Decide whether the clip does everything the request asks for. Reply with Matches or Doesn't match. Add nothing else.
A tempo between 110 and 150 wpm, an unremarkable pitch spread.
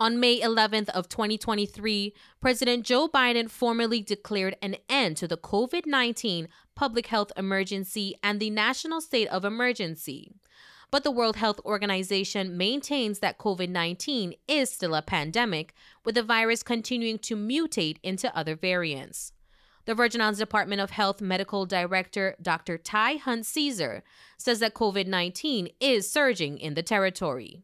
Matches